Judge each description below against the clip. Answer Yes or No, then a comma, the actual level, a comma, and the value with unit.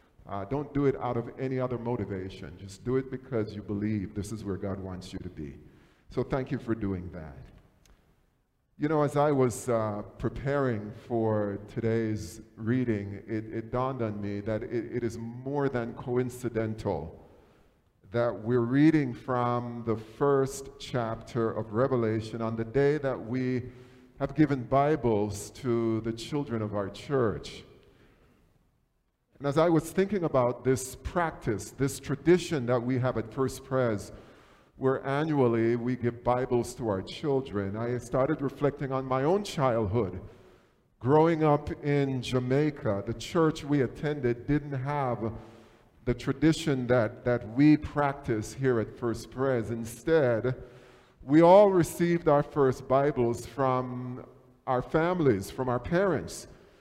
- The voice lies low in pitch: Yes, low, 125 Hz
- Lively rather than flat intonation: No, average, 3.6 semitones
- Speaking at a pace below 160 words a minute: Yes, average, 145 wpm